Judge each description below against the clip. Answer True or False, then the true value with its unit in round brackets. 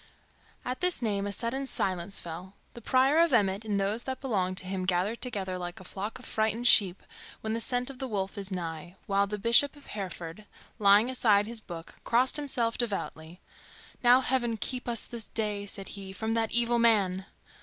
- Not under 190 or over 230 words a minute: True (195 wpm)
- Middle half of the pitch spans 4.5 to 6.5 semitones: False (3.9 semitones)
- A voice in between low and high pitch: False (215 Hz)